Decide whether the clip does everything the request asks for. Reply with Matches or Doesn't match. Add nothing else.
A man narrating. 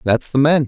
Matches